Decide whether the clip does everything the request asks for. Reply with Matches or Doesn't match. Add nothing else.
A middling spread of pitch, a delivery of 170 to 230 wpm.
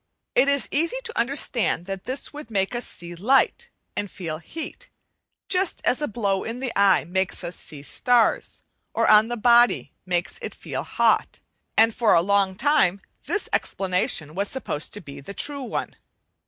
Doesn't match